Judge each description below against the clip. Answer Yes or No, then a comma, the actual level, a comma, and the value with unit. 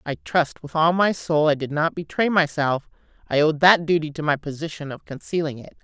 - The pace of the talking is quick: Yes, fast, 215 wpm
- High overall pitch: No, medium, 155 Hz